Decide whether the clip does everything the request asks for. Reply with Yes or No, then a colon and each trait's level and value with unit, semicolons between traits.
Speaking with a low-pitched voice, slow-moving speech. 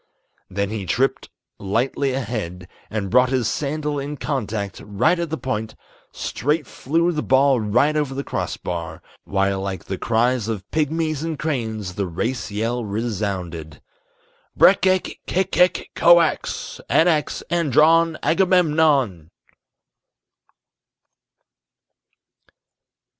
Yes: low, 130 Hz; slow, 110 wpm